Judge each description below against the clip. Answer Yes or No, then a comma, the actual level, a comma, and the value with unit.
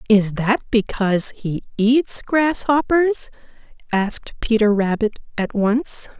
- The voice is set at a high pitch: Yes, high, 230 Hz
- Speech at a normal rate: No, slow, 105 wpm